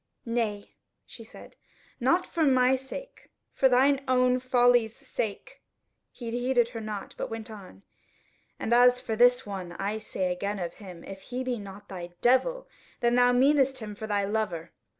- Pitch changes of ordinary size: Yes, average, 3.9 semitones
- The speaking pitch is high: Yes, high, 235 Hz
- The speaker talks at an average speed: Yes, average, 170 wpm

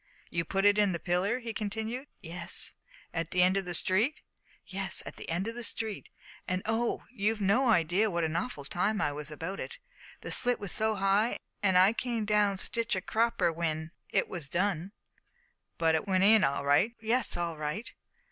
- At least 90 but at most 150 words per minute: No, average, 195 wpm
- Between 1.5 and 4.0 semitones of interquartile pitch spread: No, average, 4.4 semitones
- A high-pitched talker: Yes, high, 195 Hz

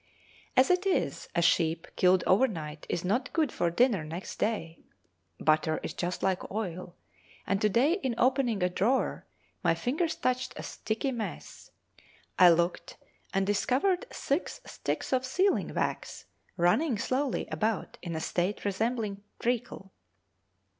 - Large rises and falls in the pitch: Yes, wide, 6.4 semitones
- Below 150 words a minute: Yes, average, 140 wpm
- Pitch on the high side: Yes, high, 215 Hz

